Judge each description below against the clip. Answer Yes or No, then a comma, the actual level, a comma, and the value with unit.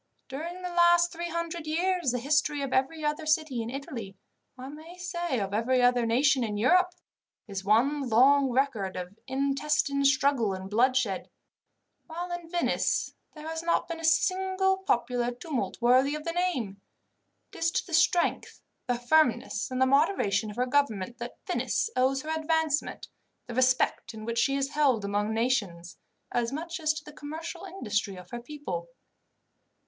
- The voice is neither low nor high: No, very high, 275 Hz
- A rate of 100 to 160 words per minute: No, average, 170 wpm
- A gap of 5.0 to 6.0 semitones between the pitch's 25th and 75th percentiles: Yes, wide, 5.4 semitones